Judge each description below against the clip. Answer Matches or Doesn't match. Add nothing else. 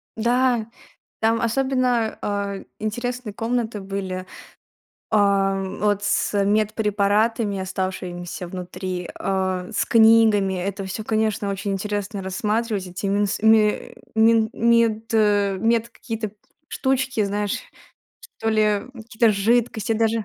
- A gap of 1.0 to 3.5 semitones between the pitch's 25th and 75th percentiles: Matches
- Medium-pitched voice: Doesn't match